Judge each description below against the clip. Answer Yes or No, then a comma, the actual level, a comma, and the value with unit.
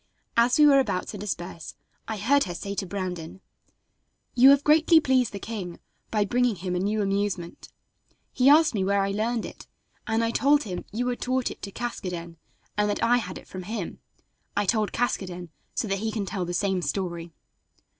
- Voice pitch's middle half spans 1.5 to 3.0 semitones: No, average, 4.7 semitones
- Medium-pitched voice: No, high, 205 Hz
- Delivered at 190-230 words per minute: Yes, average, 195 wpm